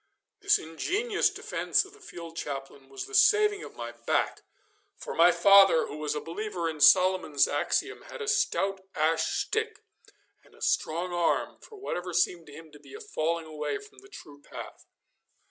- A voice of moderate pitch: Yes, medium, 170 Hz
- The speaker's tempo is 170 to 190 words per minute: Yes, average, 180 wpm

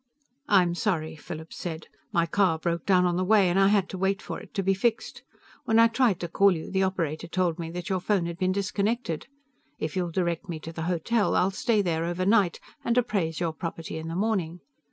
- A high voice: No, medium, 180 Hz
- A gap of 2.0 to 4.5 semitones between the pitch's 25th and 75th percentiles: Yes, average, 3.0 semitones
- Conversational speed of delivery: No, fast, 220 wpm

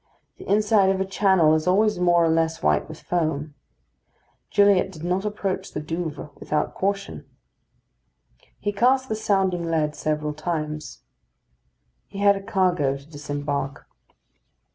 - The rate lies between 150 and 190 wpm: No, average, 140 wpm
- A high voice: No, medium, 175 Hz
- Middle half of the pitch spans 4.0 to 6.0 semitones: Yes, average, 4.5 semitones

